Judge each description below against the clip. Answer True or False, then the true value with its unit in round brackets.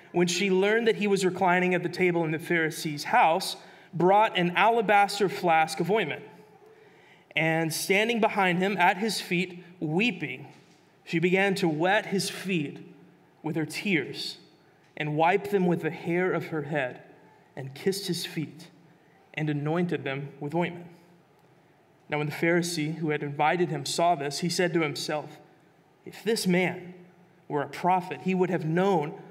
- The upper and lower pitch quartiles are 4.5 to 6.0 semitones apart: False (3.2 semitones)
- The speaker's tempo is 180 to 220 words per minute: False (160 wpm)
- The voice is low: False (175 Hz)